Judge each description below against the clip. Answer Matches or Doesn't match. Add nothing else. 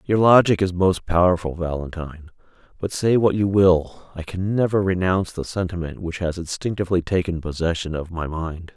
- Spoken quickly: Doesn't match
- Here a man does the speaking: Matches